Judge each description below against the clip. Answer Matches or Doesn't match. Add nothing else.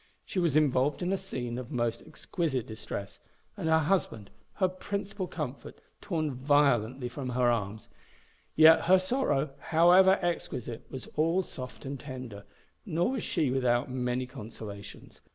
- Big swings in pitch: Matches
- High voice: Doesn't match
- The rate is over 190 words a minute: Doesn't match